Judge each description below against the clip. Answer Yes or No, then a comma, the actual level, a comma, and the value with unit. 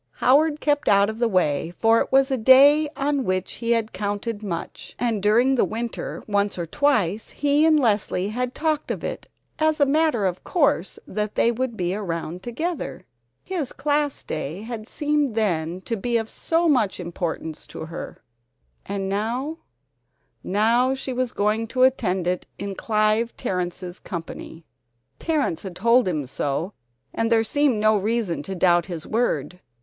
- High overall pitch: Yes, high, 220 Hz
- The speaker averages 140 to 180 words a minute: Yes, average, 165 wpm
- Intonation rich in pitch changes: Yes, wide, 5.9 semitones